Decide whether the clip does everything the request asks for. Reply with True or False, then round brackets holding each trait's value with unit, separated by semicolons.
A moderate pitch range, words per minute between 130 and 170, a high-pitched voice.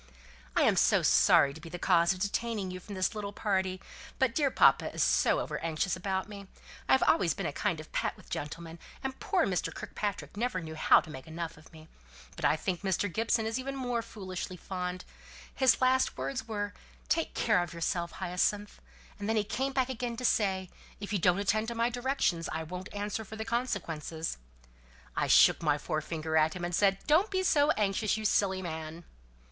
False (4.8 semitones; 205 wpm; 195 Hz)